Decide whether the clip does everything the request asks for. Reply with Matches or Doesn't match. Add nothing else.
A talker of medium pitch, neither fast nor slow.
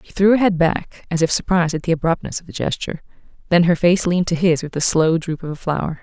Doesn't match